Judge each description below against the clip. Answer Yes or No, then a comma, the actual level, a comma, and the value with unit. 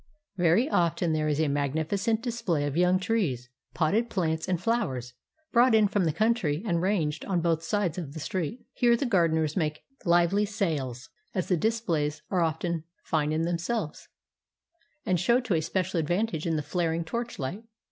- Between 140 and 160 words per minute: No, average, 170 wpm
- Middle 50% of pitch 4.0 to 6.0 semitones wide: Yes, average, 4.7 semitones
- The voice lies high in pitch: No, medium, 170 Hz